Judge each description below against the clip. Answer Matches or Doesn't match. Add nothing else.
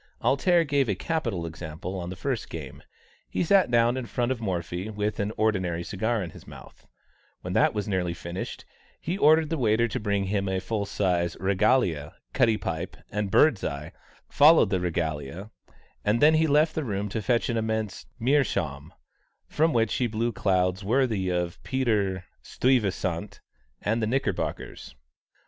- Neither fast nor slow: Matches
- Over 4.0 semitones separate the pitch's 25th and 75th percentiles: Matches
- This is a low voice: Matches